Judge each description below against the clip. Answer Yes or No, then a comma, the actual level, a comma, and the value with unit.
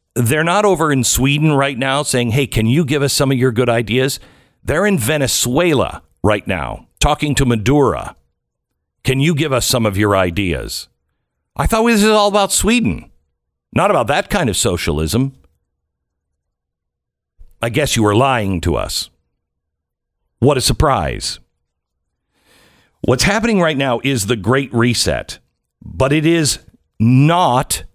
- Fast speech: No, average, 150 wpm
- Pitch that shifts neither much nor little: No, wide, 8.5 semitones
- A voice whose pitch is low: Yes, low, 125 Hz